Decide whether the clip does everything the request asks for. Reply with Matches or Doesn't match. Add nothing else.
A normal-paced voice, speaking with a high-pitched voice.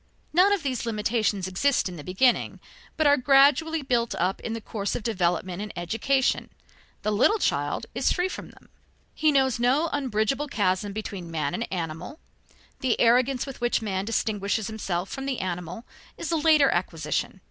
Matches